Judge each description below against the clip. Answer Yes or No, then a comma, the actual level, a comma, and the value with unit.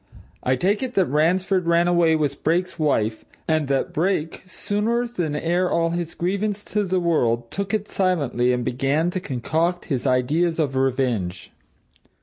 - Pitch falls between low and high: Yes, medium, 165 Hz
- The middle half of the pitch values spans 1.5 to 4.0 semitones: No, wide, 5.4 semitones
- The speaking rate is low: No, average, 160 wpm